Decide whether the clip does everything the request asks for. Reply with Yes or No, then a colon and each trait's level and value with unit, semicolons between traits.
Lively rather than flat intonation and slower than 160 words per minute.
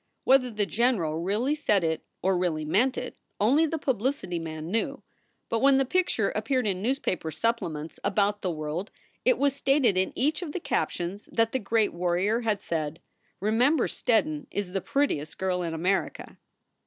No: wide, 6.9 semitones; average, 175 wpm